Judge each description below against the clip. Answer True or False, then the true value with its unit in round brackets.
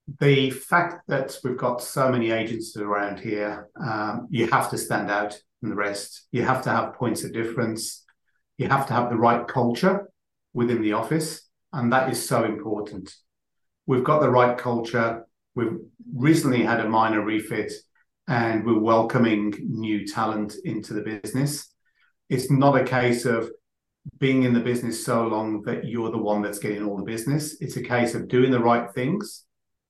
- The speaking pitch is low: True (120 Hz)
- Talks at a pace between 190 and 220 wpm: False (175 wpm)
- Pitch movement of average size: True (3.0 semitones)